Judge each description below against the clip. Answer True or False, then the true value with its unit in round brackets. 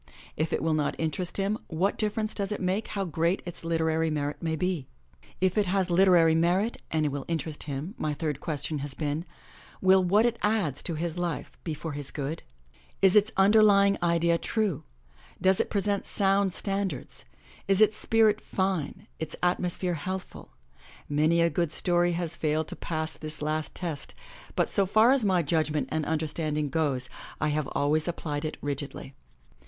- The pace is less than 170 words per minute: False (175 wpm)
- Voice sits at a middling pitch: True (170 Hz)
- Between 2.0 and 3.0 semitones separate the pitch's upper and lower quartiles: False (3.9 semitones)